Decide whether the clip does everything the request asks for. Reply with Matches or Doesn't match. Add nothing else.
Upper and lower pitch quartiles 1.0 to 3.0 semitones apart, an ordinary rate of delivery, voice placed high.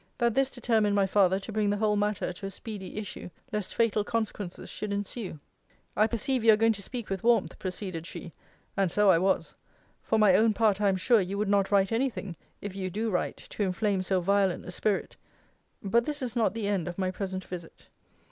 Doesn't match